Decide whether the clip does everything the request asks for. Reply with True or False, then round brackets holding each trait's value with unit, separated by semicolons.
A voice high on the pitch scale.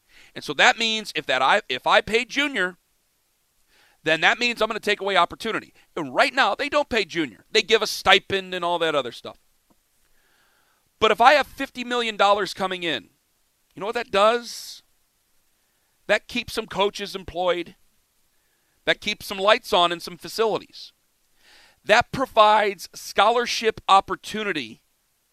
True (210 Hz)